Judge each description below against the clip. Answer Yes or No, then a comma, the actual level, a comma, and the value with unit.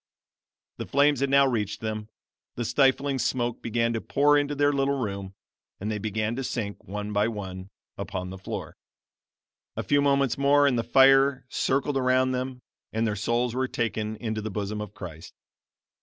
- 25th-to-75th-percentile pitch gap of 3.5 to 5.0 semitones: Yes, average, 4.4 semitones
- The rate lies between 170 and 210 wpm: Yes, average, 175 wpm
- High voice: No, low, 120 Hz